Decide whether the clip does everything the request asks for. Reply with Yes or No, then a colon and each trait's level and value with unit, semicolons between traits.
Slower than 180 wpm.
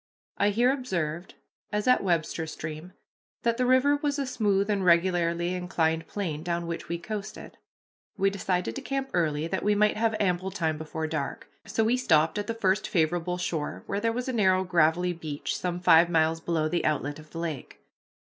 No: average, 190 wpm